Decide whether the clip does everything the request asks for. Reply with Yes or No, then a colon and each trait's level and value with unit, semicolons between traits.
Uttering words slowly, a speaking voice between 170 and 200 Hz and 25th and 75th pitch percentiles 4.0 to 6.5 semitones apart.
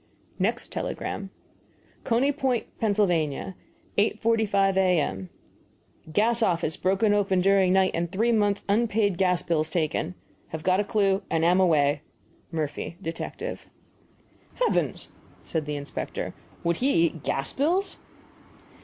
Yes: slow, 125 wpm; high, 190 Hz; average, 4.4 semitones